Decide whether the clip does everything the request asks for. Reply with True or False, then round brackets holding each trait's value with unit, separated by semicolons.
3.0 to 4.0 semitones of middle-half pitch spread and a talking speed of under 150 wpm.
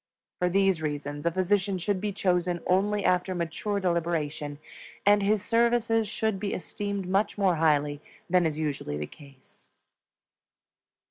False (4.4 semitones; 140 wpm)